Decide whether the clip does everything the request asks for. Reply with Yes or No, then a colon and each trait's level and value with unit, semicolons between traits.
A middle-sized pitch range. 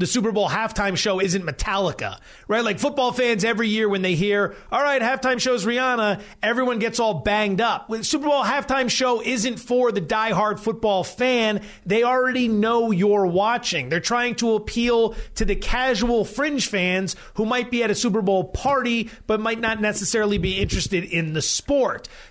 Yes: average, 3.4 semitones